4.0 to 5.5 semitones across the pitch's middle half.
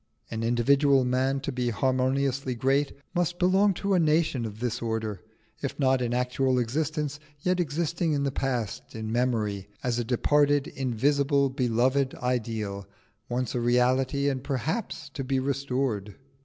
No: average, 2.8 semitones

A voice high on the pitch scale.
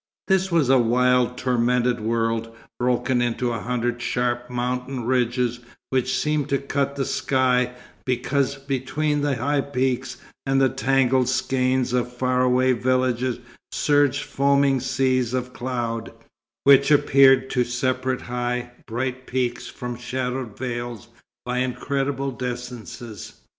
No: low, 125 Hz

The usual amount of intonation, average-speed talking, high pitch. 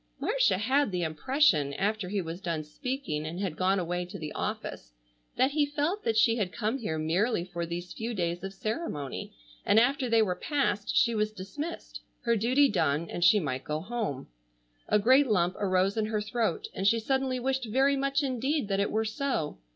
No: wide, 6.8 semitones; average, 195 wpm; high, 210 Hz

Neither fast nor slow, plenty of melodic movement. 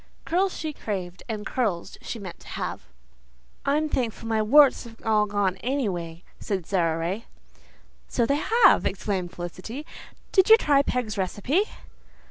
Yes: average, 150 wpm; wide, 6.9 semitones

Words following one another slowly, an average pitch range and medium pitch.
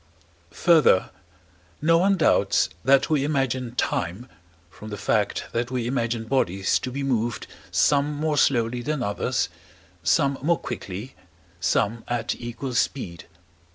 No: slow, 130 wpm; average, 3.6 semitones; low, 125 Hz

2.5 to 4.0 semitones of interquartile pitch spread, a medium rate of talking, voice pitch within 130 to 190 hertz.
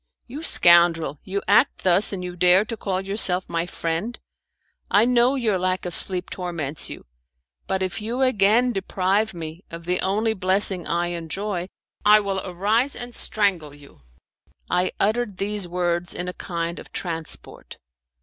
Yes: average, 3.3 semitones; average, 160 wpm; medium, 185 Hz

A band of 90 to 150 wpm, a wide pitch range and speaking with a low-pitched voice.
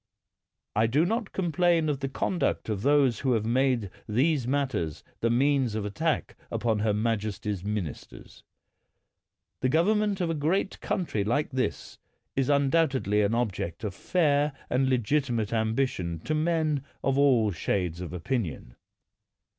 Yes: average, 145 wpm; wide, 5.8 semitones; low, 130 Hz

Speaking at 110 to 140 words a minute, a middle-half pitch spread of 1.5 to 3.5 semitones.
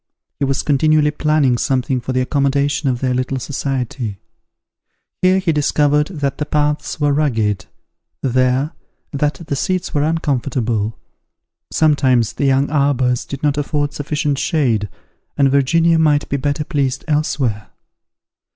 Yes: slow, 135 wpm; narrow, 2.6 semitones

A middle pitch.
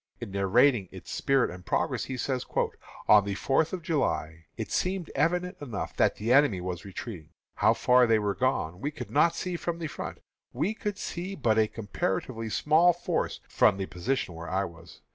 No: low, 120 Hz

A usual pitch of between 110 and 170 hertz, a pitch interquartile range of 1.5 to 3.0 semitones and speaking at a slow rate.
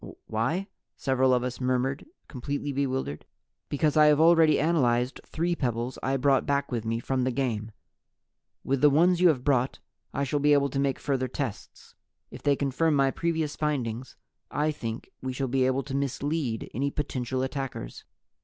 No: low, 135 Hz; narrow, 2.6 semitones; average, 175 wpm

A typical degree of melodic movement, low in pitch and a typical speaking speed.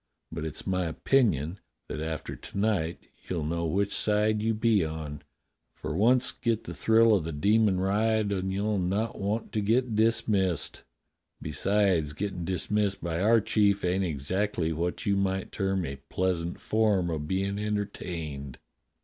Yes: average, 4.1 semitones; very low, 95 Hz; average, 155 wpm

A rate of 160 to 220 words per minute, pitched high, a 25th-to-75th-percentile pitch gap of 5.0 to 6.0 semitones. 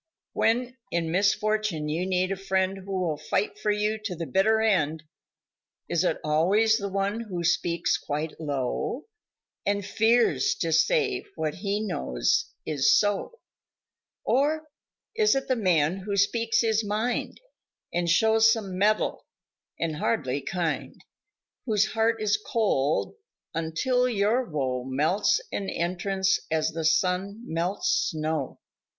No: slow, 135 wpm; high, 195 Hz; average, 5.3 semitones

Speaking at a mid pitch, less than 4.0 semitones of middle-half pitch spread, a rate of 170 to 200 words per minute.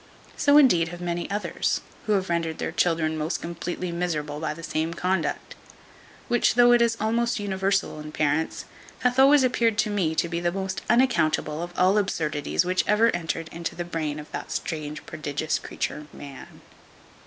No: medium, 175 Hz; average, 4.8 semitones; average, 175 wpm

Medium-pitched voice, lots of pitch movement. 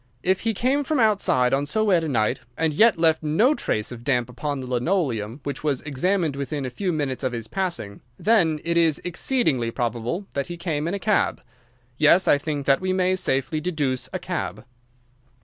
Yes: medium, 155 Hz; wide, 6.0 semitones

